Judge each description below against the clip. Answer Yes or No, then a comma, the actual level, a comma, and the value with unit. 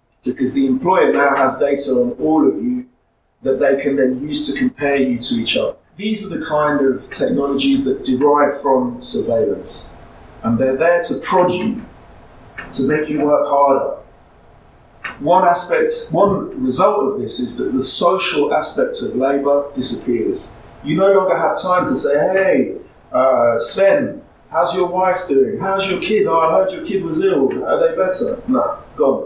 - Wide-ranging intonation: Yes, wide, 7.5 semitones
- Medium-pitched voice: Yes, medium, 150 Hz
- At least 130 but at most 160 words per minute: No, average, 175 wpm